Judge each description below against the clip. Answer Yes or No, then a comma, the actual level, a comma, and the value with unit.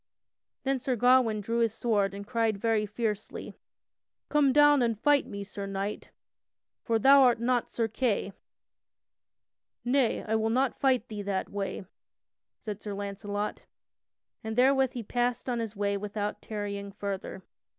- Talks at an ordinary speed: Yes, average, 150 wpm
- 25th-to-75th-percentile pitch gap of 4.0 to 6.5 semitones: No, average, 3.4 semitones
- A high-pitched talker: Yes, high, 220 Hz